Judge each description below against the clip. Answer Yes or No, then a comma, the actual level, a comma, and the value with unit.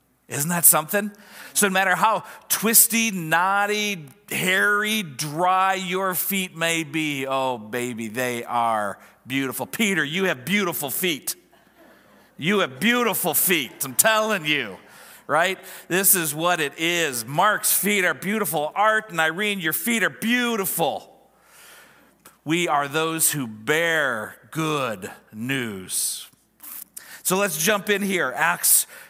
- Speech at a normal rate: No, slow, 130 wpm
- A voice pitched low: No, medium, 175 Hz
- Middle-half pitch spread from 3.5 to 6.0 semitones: Yes, wide, 5.4 semitones